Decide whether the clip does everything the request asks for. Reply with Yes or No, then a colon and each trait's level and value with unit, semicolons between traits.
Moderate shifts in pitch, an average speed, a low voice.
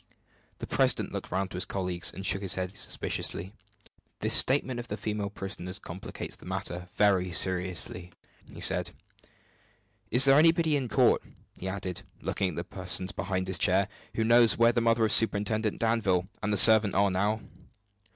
Yes: average, 3.4 semitones; average, 170 wpm; low, 100 Hz